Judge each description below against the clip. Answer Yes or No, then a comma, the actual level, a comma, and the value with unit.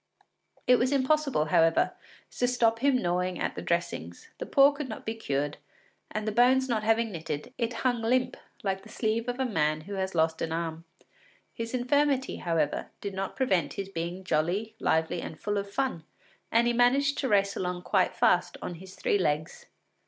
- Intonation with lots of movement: Yes, wide, 6.4 semitones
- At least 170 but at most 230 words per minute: Yes, average, 190 wpm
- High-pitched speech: Yes, high, 205 Hz